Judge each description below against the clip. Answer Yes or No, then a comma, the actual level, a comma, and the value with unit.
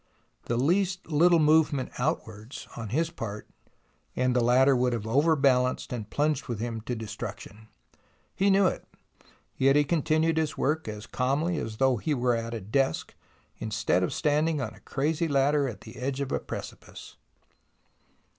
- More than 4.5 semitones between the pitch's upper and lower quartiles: Yes, average, 5.0 semitones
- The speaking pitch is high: No, low, 135 Hz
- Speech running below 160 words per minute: No, average, 170 wpm